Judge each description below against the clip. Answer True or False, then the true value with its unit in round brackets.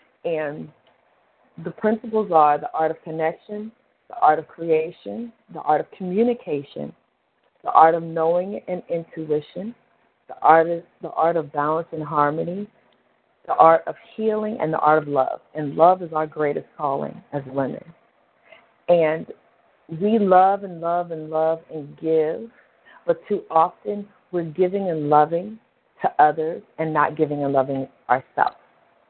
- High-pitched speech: False (165 Hz)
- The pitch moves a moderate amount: True (4.2 semitones)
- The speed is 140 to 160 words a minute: True (150 wpm)